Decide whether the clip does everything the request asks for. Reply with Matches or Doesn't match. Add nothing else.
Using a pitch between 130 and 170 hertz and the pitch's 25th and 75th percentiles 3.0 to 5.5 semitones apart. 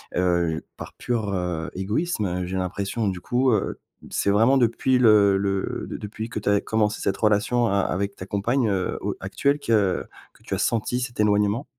Doesn't match